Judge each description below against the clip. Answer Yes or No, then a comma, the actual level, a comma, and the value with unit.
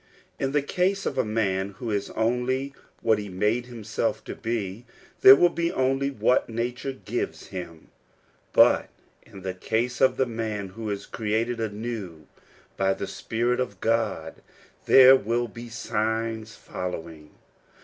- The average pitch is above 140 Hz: No, low, 115 Hz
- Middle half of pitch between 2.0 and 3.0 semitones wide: No, average, 3.4 semitones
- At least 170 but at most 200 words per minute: No, average, 150 wpm